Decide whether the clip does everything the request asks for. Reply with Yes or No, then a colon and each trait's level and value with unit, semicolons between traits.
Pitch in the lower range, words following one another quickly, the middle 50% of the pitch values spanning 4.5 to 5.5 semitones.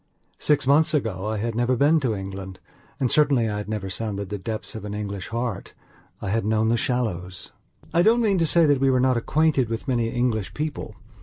Yes: low, 115 Hz; fast, 215 wpm; average, 5.0 semitones